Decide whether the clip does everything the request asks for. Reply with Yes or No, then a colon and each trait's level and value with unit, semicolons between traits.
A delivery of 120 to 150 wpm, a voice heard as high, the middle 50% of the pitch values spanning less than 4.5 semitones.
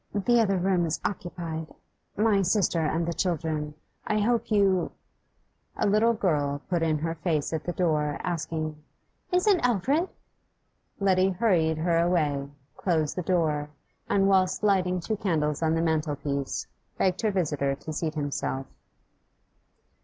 No: average, 145 wpm; medium, 170 Hz; average, 4.0 semitones